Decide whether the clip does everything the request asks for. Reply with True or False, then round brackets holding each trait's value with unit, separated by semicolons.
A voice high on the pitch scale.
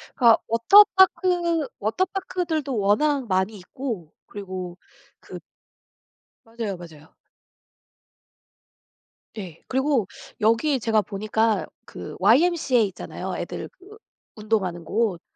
True (225 Hz)